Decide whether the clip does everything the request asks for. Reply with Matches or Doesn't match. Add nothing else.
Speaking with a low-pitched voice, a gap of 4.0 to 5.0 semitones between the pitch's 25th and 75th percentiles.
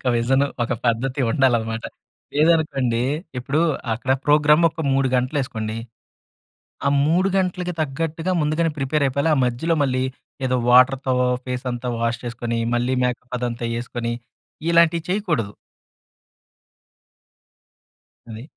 Matches